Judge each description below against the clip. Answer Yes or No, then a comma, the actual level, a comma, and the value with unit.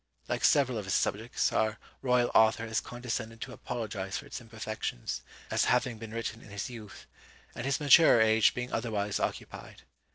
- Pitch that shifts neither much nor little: No, narrow, 2.1 semitones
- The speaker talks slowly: No, average, 170 wpm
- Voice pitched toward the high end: No, low, 115 Hz